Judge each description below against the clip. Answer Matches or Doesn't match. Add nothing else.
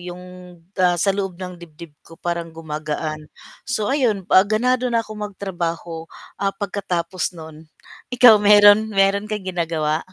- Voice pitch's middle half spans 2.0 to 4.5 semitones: Matches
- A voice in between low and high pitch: Matches